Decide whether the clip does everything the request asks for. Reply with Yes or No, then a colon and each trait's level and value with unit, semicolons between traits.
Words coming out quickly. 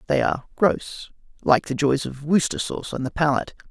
No: average, 195 wpm